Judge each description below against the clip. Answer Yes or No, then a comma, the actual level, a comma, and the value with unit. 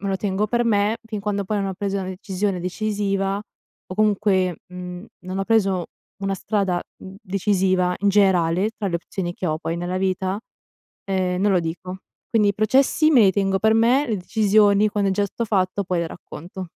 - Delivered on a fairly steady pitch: Yes, narrow, 2.1 semitones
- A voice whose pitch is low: No, high, 195 Hz